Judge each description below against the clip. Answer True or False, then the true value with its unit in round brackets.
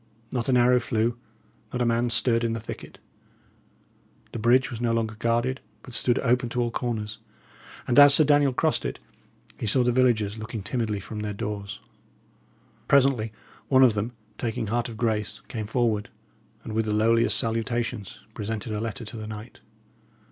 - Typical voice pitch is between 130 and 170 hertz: False (115 Hz)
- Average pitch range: False (2.1 semitones)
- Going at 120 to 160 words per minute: False (175 wpm)